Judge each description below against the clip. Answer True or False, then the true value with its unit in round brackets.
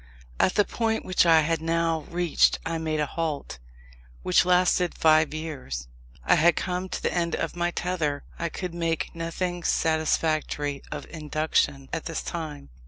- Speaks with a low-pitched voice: False (165 Hz)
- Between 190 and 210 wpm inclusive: False (165 wpm)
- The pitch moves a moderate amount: False (2.2 semitones)